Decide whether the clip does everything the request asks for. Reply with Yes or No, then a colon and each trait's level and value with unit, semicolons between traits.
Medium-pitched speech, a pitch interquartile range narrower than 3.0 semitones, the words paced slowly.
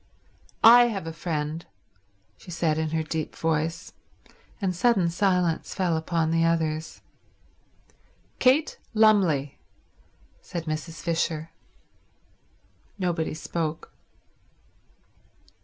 Yes: medium, 165 Hz; narrow, 2.4 semitones; slow, 90 wpm